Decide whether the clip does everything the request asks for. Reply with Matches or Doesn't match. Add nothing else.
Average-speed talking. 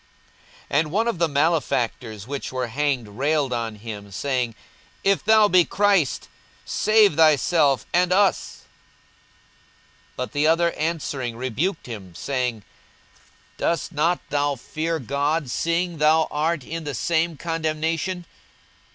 Doesn't match